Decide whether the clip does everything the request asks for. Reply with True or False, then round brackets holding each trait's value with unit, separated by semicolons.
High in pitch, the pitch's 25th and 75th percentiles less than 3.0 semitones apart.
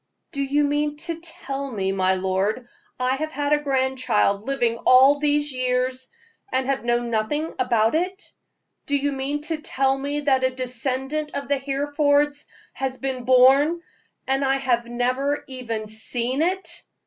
True (270 Hz; 2.5 semitones)